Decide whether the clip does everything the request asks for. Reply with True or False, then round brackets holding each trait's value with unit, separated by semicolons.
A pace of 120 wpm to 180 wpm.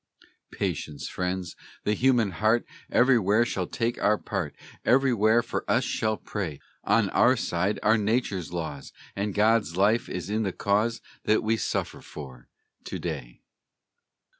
True (140 wpm)